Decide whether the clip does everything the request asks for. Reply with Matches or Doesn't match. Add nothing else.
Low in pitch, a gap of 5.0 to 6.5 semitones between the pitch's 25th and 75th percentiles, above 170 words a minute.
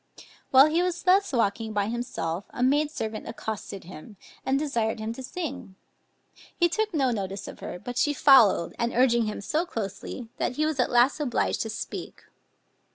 Doesn't match